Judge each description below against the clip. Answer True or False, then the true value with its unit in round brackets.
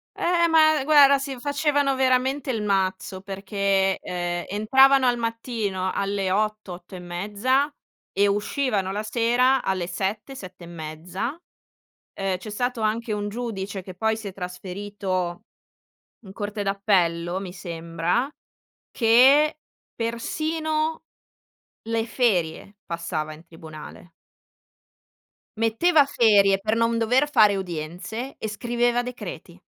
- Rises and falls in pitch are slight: False (5.0 semitones)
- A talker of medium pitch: False (210 Hz)